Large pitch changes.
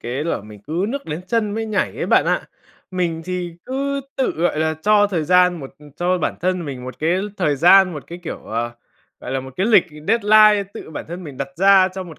No: average, 4.6 semitones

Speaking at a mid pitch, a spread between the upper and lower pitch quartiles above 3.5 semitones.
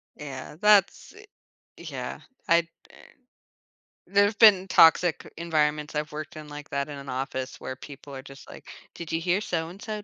Yes: medium, 155 Hz; average, 4.4 semitones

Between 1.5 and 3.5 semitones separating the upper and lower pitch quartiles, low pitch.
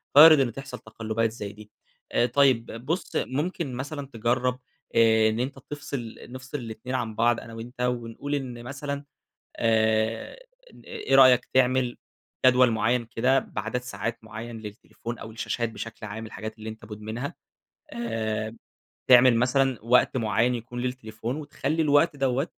Yes: average, 2.8 semitones; low, 120 Hz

